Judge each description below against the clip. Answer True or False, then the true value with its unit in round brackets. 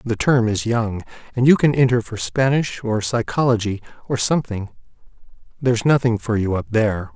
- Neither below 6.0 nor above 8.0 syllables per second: False (5.4 syllables/s)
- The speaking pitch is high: False (115 Hz)